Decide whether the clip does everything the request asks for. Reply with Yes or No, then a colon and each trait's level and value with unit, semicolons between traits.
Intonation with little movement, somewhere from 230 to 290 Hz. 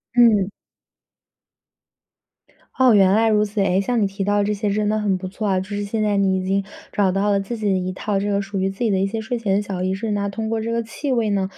No: narrow, 2.0 semitones; high, 205 Hz